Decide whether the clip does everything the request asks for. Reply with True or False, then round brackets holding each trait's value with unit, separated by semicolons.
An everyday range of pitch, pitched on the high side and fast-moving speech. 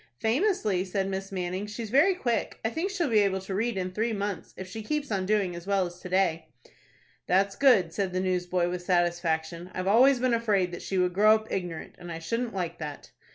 True (3.7 semitones; 195 Hz; 220 wpm)